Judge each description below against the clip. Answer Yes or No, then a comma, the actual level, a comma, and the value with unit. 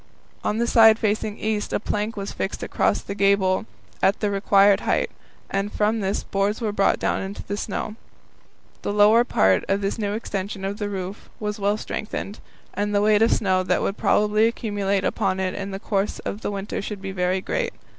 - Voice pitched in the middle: No, high, 205 Hz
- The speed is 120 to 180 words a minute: No, average, 200 wpm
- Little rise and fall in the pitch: Yes, narrow, 1.3 semitones